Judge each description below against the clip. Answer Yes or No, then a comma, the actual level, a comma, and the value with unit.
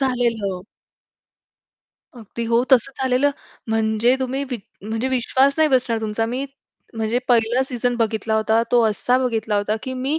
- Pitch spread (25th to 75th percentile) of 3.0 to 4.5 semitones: No, narrow, 2.6 semitones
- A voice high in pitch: Yes, high, 235 Hz